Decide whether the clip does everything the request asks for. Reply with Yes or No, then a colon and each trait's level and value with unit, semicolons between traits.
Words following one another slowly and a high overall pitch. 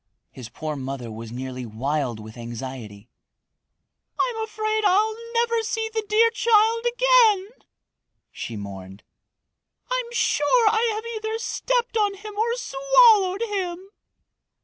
Yes: slow, 125 wpm; very high, 425 Hz